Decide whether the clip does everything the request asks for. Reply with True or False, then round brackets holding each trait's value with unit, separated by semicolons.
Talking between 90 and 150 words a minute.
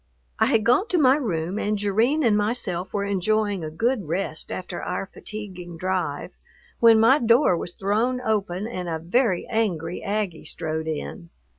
False (165 wpm)